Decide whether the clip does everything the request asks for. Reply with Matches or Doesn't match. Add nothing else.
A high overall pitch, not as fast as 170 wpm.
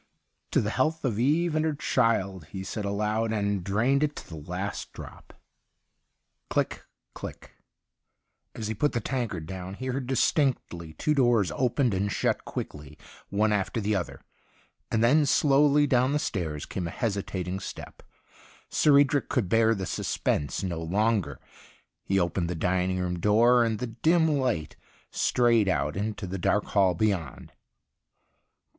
Doesn't match